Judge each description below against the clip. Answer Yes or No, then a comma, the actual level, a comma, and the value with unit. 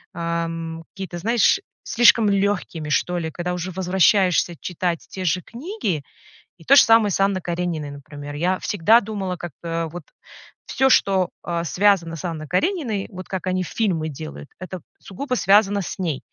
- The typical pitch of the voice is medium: Yes, medium, 180 Hz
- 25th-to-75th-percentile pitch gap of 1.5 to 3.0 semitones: No, average, 3.4 semitones